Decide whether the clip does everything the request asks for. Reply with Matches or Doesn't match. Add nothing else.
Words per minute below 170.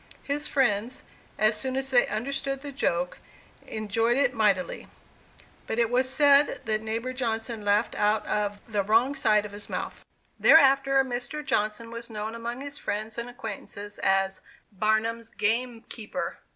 Matches